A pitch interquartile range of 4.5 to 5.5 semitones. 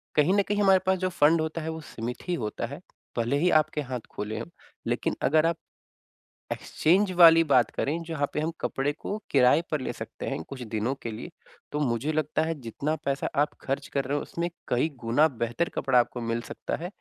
Yes: average, 4.9 semitones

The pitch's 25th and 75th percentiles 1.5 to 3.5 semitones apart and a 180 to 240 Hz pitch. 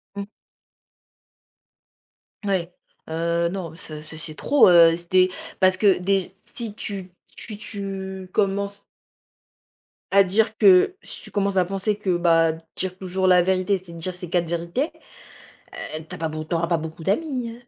Yes: average, 2.8 semitones; medium, 185 Hz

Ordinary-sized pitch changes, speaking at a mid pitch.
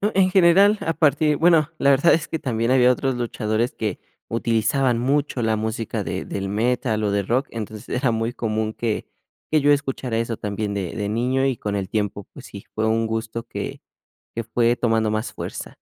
No: average, 3.6 semitones; low, 115 Hz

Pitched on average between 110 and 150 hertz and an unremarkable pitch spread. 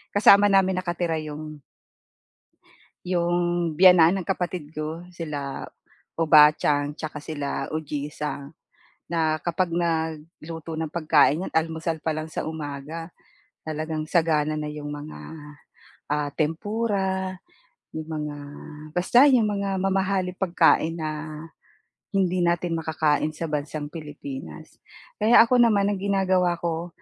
No: medium, 165 Hz; average, 3.1 semitones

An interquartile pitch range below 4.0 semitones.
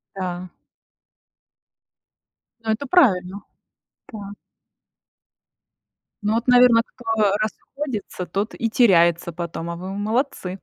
No: average, 4.3 semitones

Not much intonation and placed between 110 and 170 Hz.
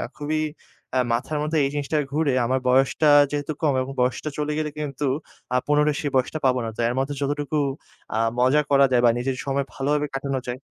Yes: narrow, 2.3 semitones; medium, 140 Hz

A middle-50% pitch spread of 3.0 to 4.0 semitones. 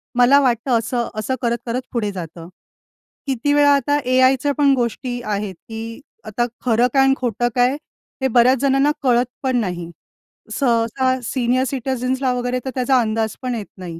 No: narrow, 2.4 semitones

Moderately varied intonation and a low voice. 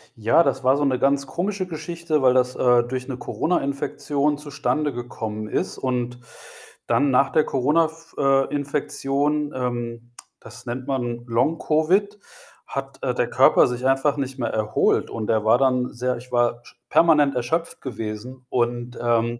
Yes: average, 3.2 semitones; low, 130 Hz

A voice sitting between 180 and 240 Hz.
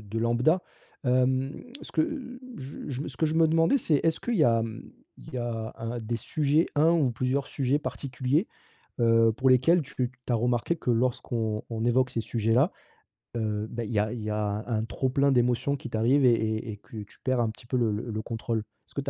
No: low, 125 Hz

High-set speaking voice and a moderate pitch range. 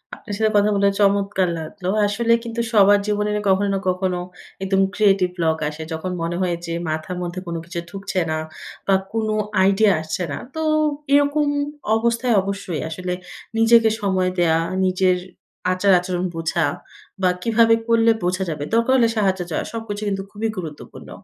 Yes: high, 195 Hz; average, 3.3 semitones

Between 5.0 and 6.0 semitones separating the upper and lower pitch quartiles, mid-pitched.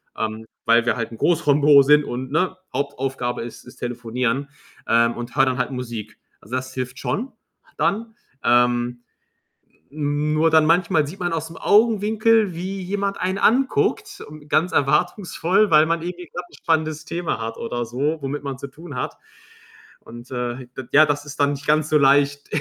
Yes: wide, 5.4 semitones; medium, 145 Hz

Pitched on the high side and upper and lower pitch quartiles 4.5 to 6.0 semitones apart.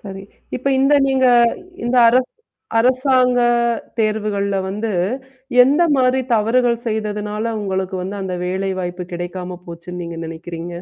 Yes: high, 210 Hz; average, 5.1 semitones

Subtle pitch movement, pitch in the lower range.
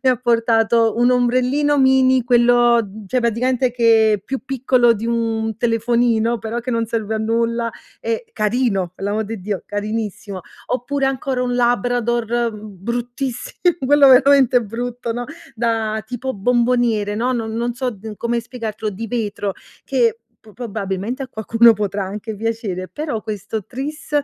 No: narrow, 2.2 semitones; high, 235 Hz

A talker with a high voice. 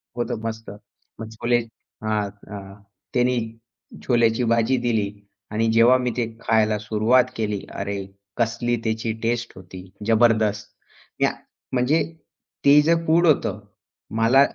No: low, 115 Hz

